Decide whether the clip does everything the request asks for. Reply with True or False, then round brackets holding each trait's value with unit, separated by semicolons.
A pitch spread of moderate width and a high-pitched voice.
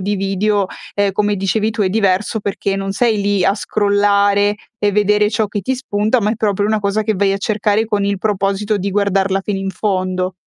False (1.3 semitones; 205 Hz)